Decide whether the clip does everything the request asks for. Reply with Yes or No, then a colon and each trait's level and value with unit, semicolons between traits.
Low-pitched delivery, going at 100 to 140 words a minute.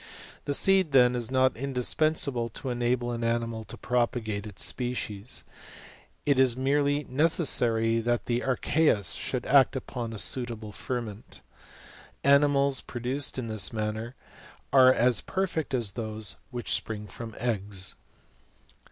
Yes: low, 120 Hz; slow, 135 wpm